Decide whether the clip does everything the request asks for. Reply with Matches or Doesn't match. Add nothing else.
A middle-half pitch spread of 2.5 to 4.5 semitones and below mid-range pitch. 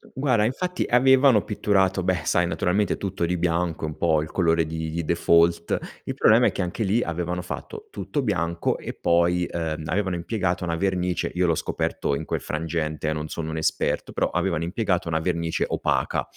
Matches